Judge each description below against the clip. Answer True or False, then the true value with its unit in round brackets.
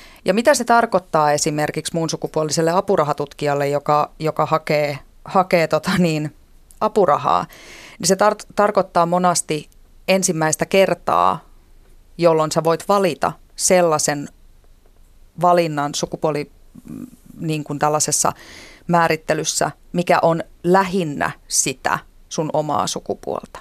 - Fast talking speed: False (100 wpm)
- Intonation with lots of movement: False (3.4 semitones)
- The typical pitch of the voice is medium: True (160 Hz)